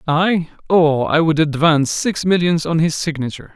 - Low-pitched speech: No, medium, 160 Hz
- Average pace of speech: Yes, average, 170 wpm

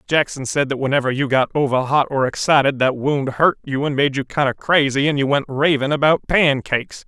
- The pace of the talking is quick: Yes, fast, 210 wpm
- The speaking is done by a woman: No, male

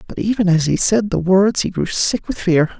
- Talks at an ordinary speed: No, fast, 255 wpm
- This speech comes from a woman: Yes, female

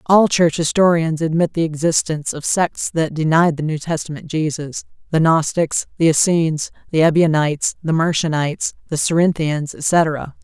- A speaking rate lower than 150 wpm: Yes, average, 140 wpm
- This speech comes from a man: No, female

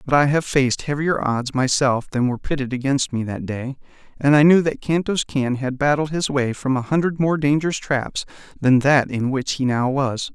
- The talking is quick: Yes, fast, 215 wpm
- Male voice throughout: Yes, male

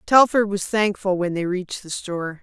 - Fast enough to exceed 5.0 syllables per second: Yes, 5.2 syllables/s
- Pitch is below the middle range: No, high, 190 Hz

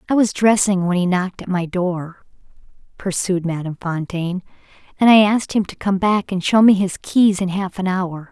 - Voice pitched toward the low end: No, high, 190 Hz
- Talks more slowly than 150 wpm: No, average, 200 wpm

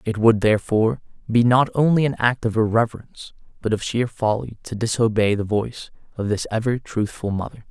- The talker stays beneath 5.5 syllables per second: No, 5.7 syllables/s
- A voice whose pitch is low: Yes, low, 115 Hz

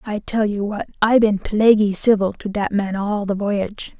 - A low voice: No, high, 205 Hz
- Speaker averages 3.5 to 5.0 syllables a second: Yes, 4.7 syllables/s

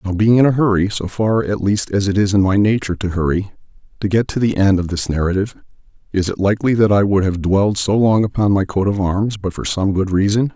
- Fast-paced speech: Yes, fast, 245 wpm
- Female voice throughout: No, male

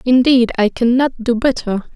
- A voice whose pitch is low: No, high, 240 Hz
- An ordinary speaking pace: Yes, average, 185 wpm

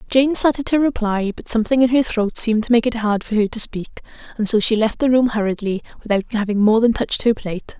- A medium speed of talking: No, fast, 245 wpm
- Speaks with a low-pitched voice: No, high, 225 Hz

